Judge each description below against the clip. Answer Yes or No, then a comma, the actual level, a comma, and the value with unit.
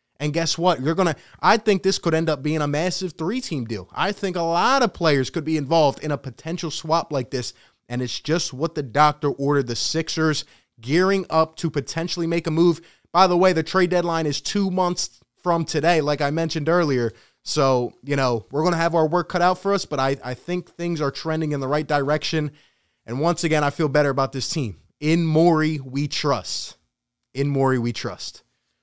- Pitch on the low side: No, medium, 155 Hz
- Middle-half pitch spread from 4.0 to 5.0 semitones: No, average, 3.5 semitones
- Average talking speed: No, fast, 215 wpm